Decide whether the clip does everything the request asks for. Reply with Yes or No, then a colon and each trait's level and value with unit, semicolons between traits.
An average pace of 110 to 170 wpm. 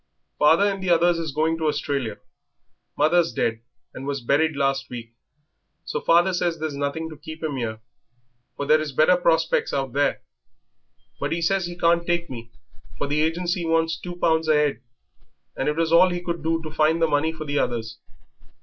No: average, 195 wpm